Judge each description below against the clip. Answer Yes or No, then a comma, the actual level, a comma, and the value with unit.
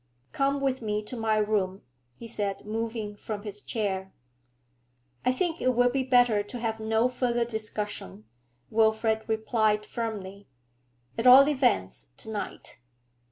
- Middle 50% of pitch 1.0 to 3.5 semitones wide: Yes, average, 2.8 semitones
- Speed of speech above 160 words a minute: No, average, 140 wpm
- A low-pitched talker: No, high, 220 Hz